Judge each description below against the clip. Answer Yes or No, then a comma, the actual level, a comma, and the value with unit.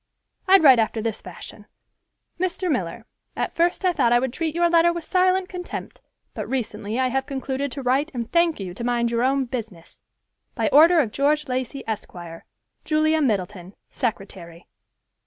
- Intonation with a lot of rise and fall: Yes, wide, 6.3 semitones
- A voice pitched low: No, very high, 260 Hz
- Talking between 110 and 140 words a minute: No, average, 160 wpm